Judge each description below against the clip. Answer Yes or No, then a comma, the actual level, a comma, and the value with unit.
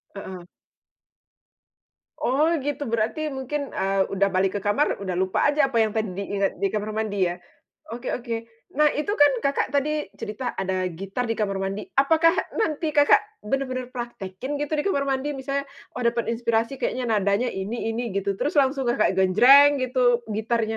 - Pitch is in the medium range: No, high, 240 Hz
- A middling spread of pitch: No, wide, 5.7 semitones